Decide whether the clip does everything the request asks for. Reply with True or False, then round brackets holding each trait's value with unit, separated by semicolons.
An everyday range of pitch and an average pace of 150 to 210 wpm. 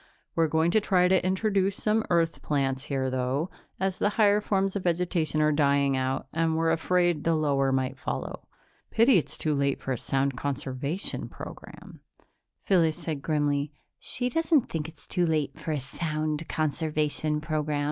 True (4.1 semitones; 165 wpm)